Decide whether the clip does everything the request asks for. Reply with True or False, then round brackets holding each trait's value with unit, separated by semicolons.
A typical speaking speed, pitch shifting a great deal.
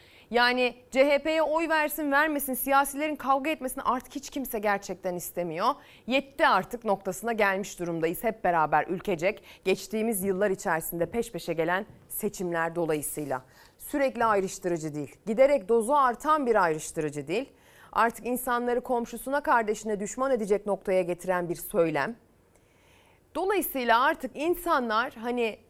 True (120 wpm; 6.5 semitones)